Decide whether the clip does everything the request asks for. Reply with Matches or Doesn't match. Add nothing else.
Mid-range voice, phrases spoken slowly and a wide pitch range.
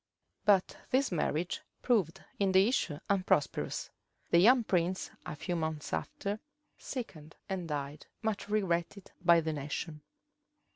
Doesn't match